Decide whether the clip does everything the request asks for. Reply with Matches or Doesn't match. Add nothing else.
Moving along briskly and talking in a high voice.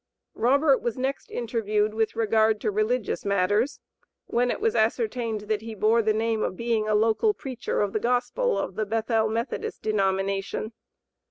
Doesn't match